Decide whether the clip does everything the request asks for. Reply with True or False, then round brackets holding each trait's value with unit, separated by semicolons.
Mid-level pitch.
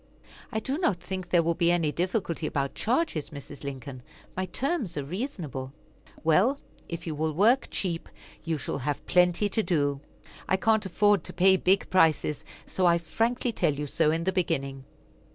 True (170 Hz)